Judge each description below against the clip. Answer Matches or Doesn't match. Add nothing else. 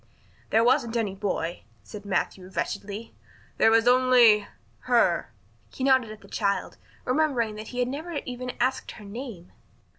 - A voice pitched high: Matches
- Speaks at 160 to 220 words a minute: Doesn't match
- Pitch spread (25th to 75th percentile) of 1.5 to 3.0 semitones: Doesn't match